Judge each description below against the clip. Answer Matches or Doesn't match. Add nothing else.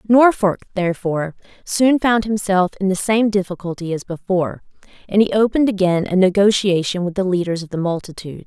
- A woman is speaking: Matches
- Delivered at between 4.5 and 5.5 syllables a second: Doesn't match